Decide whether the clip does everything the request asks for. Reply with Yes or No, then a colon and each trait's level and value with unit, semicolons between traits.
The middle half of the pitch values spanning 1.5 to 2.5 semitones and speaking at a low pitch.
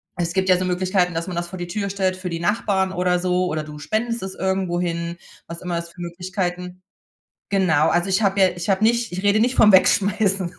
No: narrow, 1.9 semitones; medium, 185 Hz